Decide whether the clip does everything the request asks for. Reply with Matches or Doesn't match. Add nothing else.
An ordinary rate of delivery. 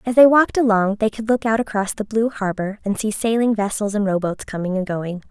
Doesn't match